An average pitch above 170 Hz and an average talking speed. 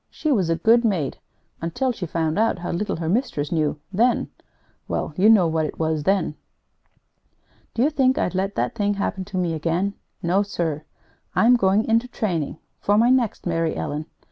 Yes: high, 190 Hz; average, 185 wpm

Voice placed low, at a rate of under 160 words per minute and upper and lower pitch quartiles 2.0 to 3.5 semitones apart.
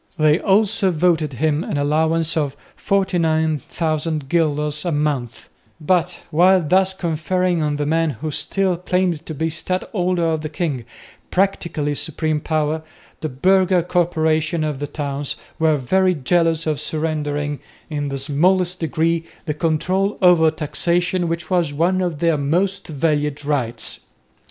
No: medium, 160 Hz; average, 140 wpm; average, 2.9 semitones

